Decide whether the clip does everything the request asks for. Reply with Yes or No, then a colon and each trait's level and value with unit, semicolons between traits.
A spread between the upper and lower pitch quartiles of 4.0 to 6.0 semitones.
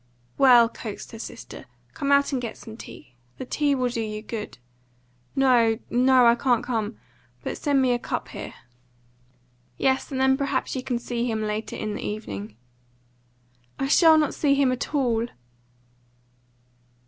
No: average, 3.2 semitones